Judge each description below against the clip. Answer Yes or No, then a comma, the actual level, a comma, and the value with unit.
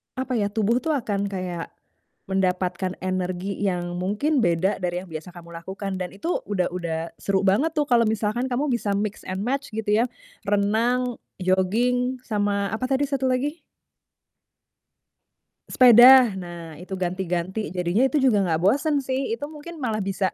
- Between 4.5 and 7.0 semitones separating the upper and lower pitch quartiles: Yes, average, 5.3 semitones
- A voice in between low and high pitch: No, high, 205 Hz